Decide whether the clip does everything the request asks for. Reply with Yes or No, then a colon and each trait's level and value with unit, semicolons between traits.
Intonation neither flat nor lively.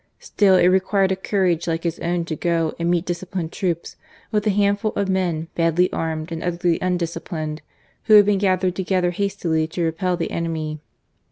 No: narrow, 2.3 semitones